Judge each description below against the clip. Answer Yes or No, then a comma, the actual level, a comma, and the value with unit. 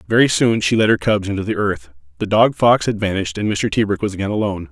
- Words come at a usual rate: No, fast, 255 wpm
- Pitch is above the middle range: No, low, 100 Hz